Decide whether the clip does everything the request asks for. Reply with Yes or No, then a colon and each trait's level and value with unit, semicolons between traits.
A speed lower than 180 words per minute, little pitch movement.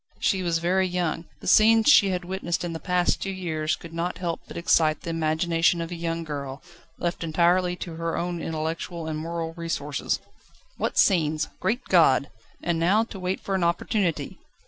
No: average, 185 wpm; narrow, 1.8 semitones